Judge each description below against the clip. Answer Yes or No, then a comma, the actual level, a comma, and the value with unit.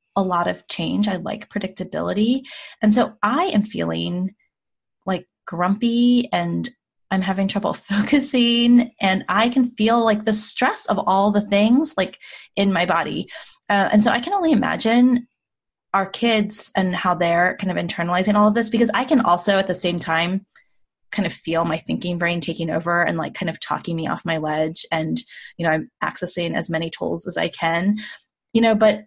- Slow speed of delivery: No, average, 190 wpm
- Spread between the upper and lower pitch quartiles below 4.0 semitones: No, average, 4.5 semitones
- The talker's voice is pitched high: Yes, high, 195 Hz